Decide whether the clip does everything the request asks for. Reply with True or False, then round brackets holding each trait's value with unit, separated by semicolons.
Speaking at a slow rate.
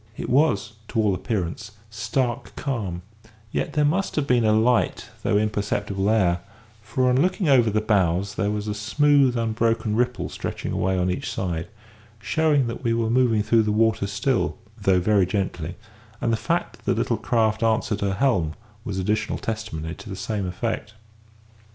False (175 wpm)